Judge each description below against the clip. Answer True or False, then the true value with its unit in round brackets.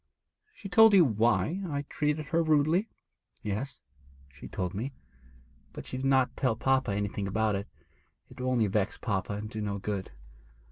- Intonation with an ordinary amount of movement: False (6.1 semitones)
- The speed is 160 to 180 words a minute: True (170 wpm)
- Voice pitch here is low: True (125 Hz)